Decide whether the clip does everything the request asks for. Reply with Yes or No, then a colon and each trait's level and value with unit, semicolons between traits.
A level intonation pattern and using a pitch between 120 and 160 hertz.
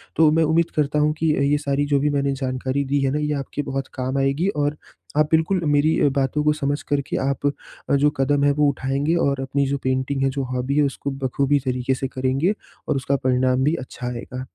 Yes: narrow, 1.8 semitones; medium, 140 Hz